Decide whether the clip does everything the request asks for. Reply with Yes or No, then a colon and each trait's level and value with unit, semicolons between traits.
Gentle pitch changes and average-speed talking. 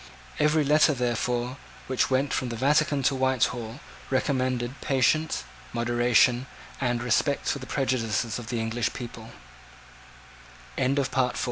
No: narrow, 2.3 semitones; slow, 115 wpm